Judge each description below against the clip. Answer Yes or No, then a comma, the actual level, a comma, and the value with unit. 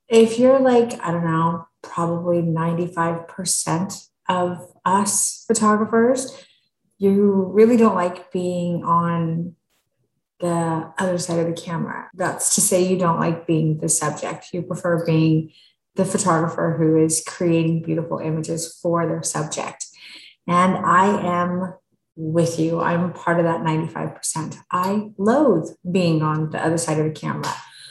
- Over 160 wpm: No, average, 140 wpm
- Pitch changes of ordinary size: No, narrow, 2.3 semitones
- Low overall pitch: No, medium, 175 Hz